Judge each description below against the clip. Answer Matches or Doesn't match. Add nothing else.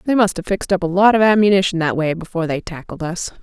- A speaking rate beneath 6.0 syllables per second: Doesn't match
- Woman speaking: Matches